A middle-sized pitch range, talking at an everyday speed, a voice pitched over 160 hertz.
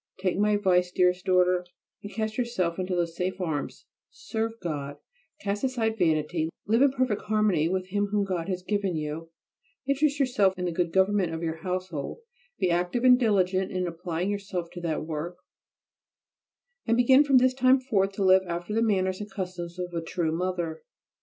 Yes: average, 3.4 semitones; average, 180 wpm; medium, 185 Hz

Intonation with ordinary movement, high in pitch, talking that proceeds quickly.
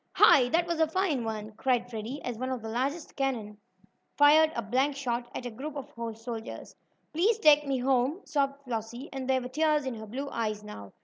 Yes: average, 4.0 semitones; very high, 260 Hz; fast, 210 wpm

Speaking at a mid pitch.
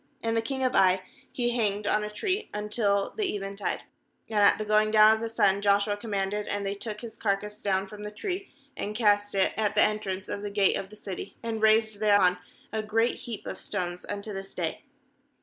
No: high, 210 Hz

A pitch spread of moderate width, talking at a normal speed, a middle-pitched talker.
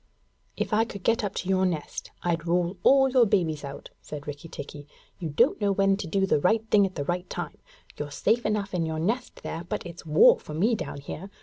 No: average, 4.4 semitones; fast, 230 wpm; medium, 180 Hz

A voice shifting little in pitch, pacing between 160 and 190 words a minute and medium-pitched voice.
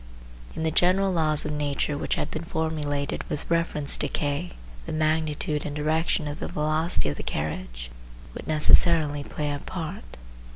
Yes: narrow, 1.9 semitones; average, 165 wpm; medium, 150 Hz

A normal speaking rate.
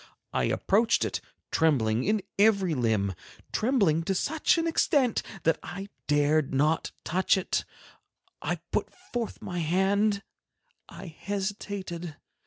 No: slow, 120 wpm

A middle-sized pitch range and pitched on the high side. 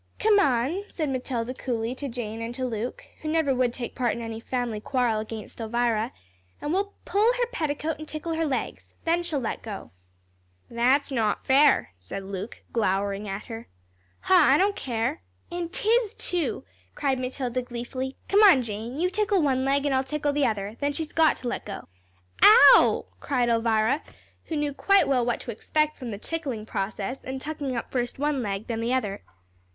Yes: average, 4.9 semitones; very high, 255 Hz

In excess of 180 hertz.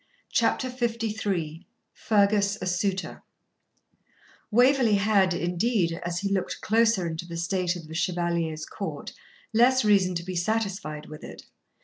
Yes: high, 190 Hz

